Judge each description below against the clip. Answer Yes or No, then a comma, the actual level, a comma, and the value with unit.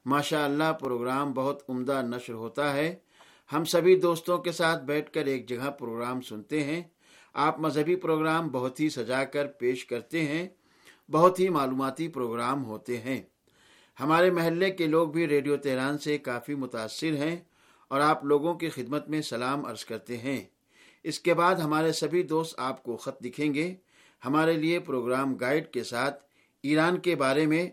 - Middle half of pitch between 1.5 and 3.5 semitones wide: No, average, 3.9 semitones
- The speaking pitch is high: No, medium, 145 Hz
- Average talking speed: Yes, average, 170 wpm